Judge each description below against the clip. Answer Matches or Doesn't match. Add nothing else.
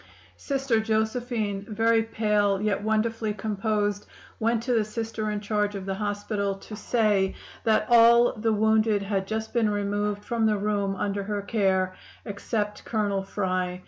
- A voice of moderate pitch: Doesn't match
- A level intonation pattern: Matches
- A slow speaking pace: Doesn't match